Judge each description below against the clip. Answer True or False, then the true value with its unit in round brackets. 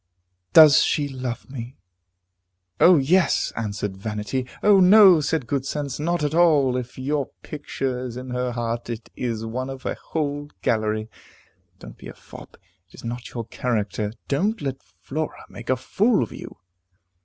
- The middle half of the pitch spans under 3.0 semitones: False (4.2 semitones)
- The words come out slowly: False (165 wpm)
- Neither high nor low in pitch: False (130 Hz)